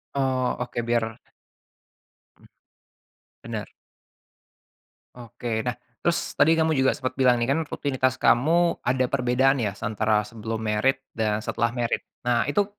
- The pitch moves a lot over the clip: No, average, 2.8 semitones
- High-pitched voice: No, low, 125 Hz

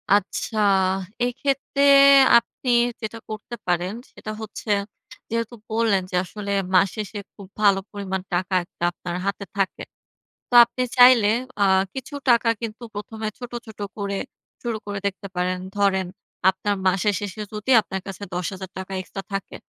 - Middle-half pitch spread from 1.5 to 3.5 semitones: Yes, average, 2.9 semitones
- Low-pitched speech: No, high, 205 Hz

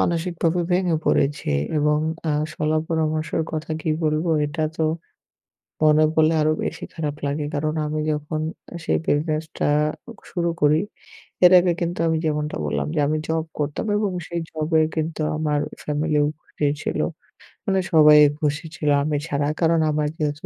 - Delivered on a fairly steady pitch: Yes, narrow, 1.5 semitones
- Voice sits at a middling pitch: Yes, medium, 155 Hz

